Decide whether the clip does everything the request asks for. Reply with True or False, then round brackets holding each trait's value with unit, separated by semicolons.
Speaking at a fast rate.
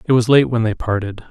True (275 wpm)